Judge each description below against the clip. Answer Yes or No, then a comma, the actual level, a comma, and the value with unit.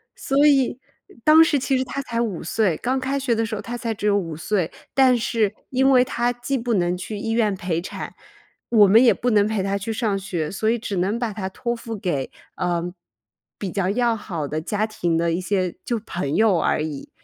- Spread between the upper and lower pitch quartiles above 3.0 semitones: Yes, average, 4.7 semitones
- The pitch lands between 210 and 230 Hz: Yes, high, 215 Hz